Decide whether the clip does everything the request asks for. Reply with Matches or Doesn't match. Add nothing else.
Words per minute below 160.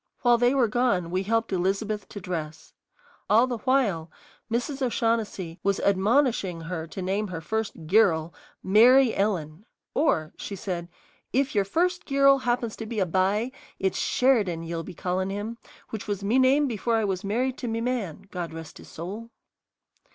Doesn't match